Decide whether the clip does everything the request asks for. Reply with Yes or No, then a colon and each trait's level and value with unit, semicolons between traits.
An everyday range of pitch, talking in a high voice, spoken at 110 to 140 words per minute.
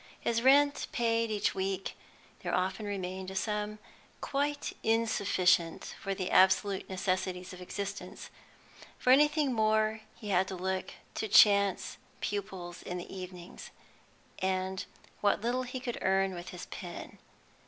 Yes: average, 3.1 semitones; high, 195 Hz; slow, 135 wpm